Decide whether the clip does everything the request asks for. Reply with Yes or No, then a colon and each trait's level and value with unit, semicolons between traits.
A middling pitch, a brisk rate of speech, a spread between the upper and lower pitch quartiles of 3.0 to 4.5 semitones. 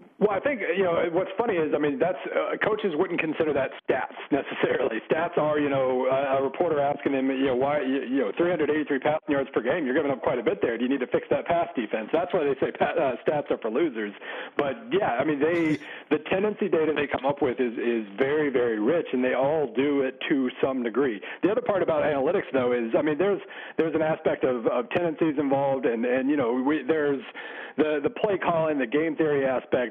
Yes: medium, 150 Hz; fast, 235 wpm; average, 4.1 semitones